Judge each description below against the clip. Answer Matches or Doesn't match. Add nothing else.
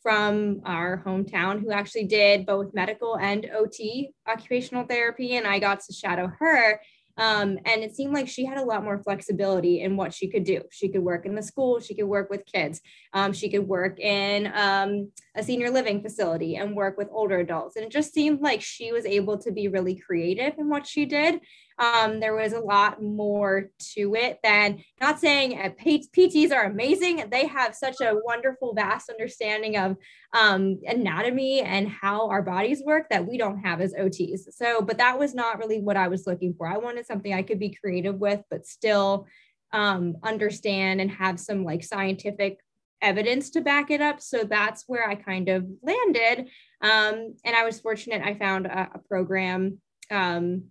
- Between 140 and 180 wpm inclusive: Doesn't match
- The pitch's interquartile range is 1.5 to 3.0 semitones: Doesn't match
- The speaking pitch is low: Doesn't match